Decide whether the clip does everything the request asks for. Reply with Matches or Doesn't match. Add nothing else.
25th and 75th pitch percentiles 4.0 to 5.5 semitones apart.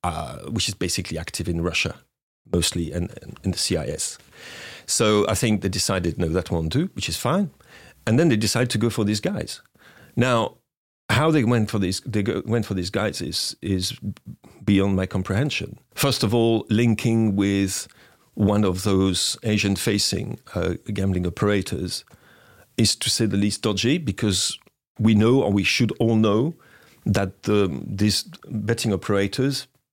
Doesn't match